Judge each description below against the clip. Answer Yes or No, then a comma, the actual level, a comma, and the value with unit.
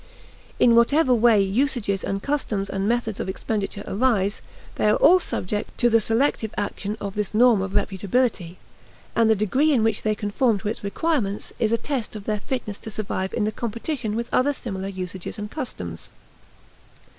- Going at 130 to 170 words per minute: No, average, 180 wpm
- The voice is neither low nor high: No, high, 215 Hz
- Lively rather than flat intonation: No, average, 3.4 semitones